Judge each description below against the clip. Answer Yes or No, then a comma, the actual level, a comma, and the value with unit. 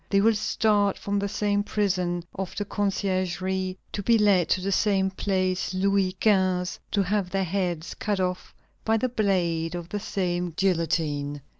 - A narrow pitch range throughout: Yes, narrow, 2.1 semitones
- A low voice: No, high, 190 Hz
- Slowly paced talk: No, average, 165 wpm